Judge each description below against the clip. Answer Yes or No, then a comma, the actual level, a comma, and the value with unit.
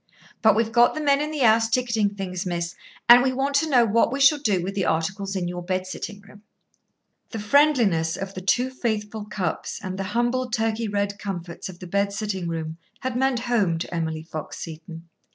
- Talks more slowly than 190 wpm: No, fast, 205 wpm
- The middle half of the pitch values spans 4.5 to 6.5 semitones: Yes, average, 4.9 semitones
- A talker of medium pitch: No, high, 205 Hz